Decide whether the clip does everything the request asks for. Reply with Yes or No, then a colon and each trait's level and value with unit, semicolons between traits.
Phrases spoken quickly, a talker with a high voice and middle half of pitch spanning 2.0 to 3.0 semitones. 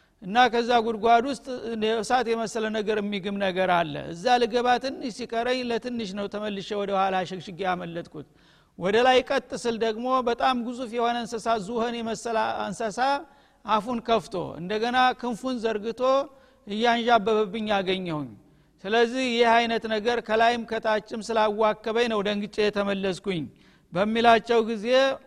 Yes: fast, 125 wpm; high, 230 Hz; average, 2.7 semitones